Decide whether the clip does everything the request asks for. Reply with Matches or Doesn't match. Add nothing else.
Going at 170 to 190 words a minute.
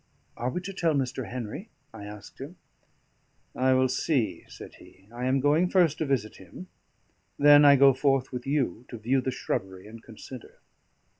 Matches